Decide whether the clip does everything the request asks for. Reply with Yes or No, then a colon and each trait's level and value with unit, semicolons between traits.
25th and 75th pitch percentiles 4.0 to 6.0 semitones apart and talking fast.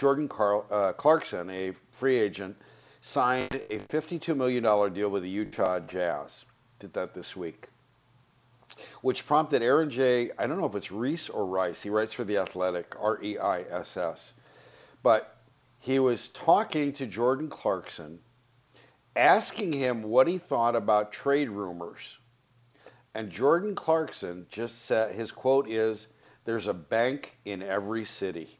No: average, 4.6 semitones; average, 150 wpm